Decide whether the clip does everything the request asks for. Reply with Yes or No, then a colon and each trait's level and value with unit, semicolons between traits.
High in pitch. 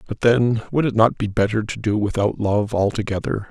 No: low, 110 Hz